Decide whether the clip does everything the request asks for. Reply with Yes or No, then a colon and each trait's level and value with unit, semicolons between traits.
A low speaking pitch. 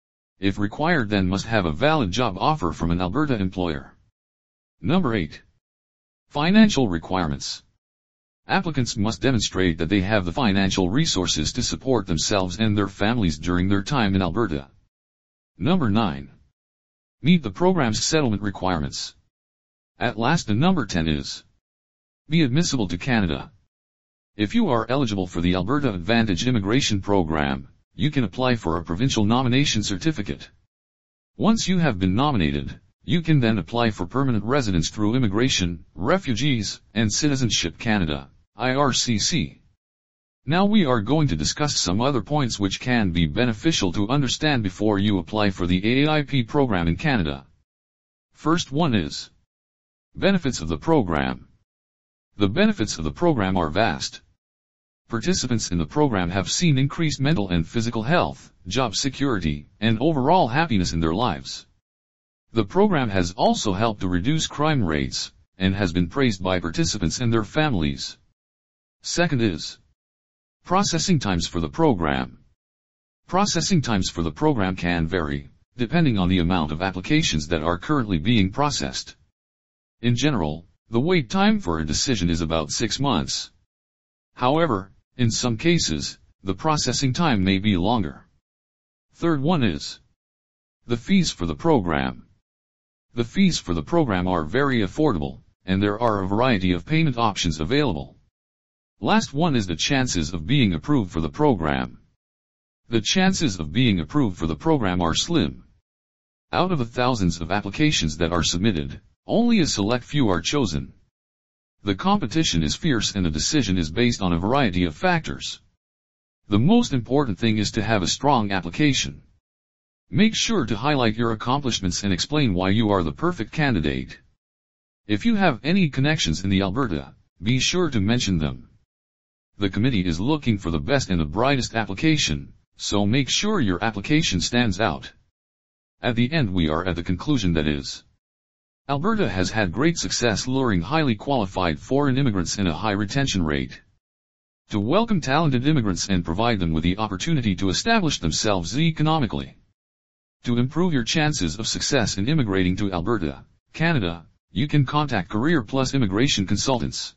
Yes: low, 100 Hz